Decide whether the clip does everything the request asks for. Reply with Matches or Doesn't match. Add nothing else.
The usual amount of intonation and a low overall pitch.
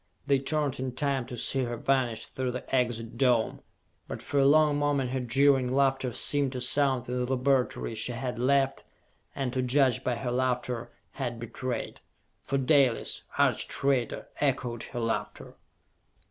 Doesn't match